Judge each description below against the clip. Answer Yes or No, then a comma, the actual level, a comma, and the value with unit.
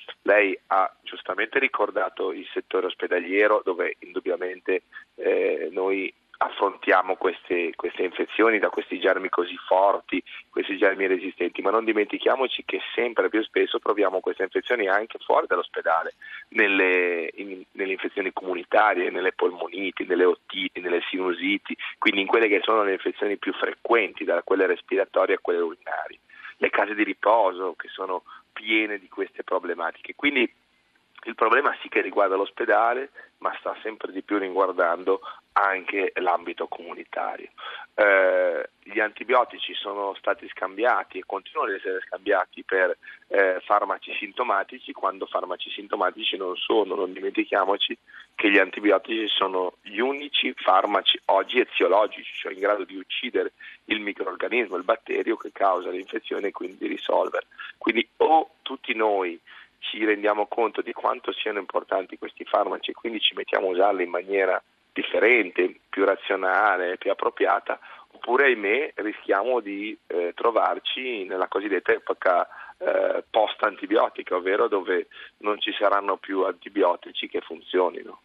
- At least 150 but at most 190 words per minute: No, average, 140 wpm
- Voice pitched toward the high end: Yes, very high, 400 Hz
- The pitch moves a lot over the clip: No, average, 3.9 semitones